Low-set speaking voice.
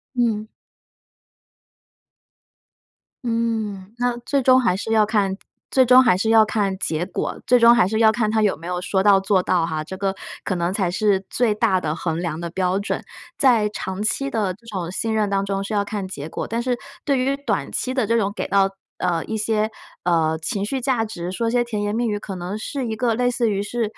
No: high, 210 Hz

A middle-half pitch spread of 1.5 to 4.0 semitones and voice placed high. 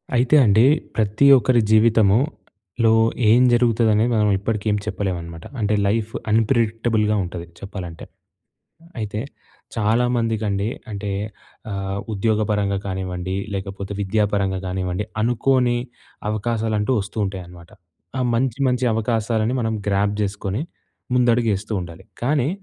No: average, 2.8 semitones; low, 105 Hz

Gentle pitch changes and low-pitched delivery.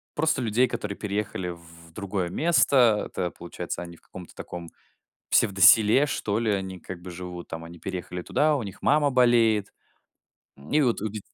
No: average, 5.1 semitones; low, 100 Hz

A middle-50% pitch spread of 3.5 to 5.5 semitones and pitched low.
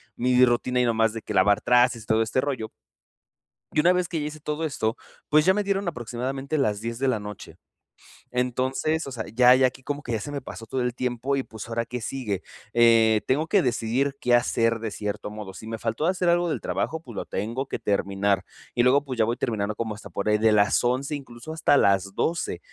Yes: average, 3.9 semitones; low, 125 Hz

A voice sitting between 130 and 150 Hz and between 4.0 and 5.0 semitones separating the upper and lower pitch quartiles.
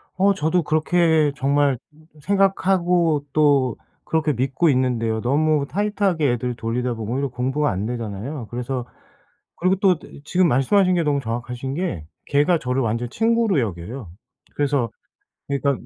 No: medium, 140 Hz; wide, 5.5 semitones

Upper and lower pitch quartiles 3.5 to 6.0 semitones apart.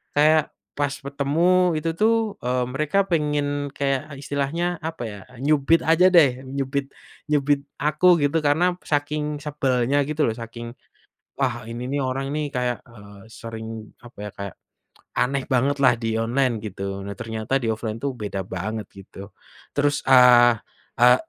Yes: average, 4.2 semitones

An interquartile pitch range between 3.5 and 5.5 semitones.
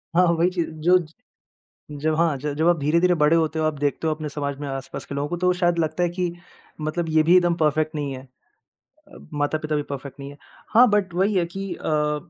No: average, 2.9 semitones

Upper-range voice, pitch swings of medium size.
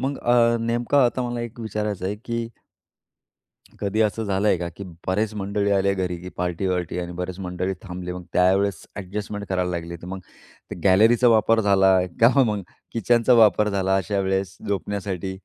No: low, 100 Hz; average, 3.0 semitones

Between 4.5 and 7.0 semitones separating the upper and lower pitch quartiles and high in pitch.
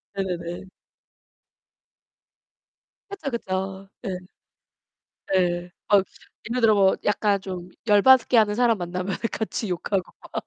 No: average, 2.9 semitones; high, 195 Hz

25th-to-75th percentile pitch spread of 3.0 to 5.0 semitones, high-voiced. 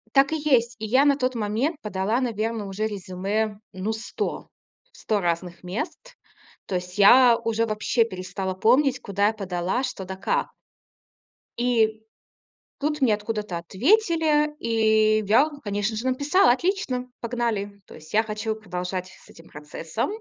Yes: average, 4.5 semitones; high, 220 Hz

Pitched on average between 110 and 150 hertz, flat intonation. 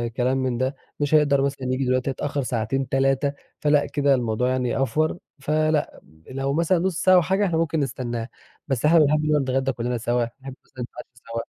No: low, 135 Hz; average, 3.0 semitones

